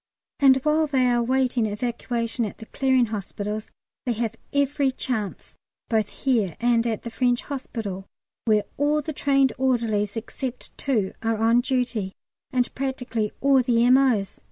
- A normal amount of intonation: Yes, average, 3.2 semitones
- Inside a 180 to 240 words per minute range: No, average, 150 wpm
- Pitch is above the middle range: Yes, high, 240 Hz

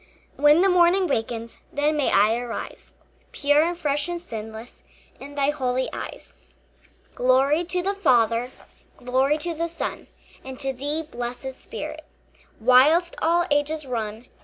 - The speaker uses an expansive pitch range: No, average, 4.6 semitones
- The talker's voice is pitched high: Yes, very high, 280 Hz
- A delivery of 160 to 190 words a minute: No, average, 140 wpm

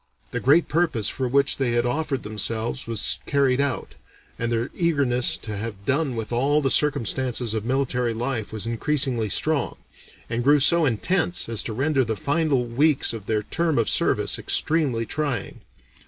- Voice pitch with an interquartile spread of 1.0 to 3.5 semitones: No, average, 4.0 semitones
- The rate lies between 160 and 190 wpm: Yes, average, 170 wpm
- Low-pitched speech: Yes, low, 125 Hz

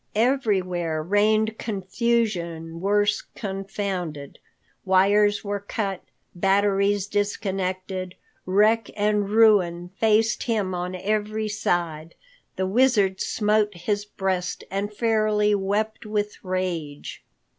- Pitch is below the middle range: No, high, 200 Hz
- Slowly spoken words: Yes, slow, 95 wpm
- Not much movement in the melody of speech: Yes, narrow, 2.3 semitones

